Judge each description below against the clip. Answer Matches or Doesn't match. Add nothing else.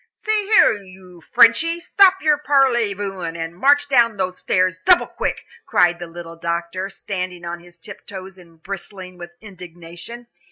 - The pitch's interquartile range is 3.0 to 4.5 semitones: Doesn't match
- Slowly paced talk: Doesn't match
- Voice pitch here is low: Doesn't match